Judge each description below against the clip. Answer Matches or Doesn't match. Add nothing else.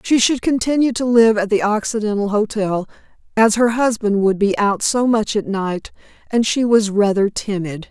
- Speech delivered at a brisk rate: Doesn't match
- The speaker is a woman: Matches